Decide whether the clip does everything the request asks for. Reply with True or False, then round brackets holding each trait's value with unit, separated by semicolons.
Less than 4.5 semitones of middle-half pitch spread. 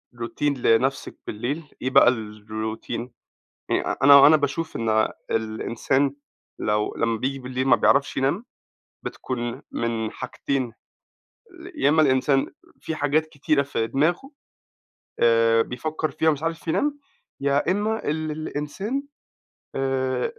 False (4.8 semitones)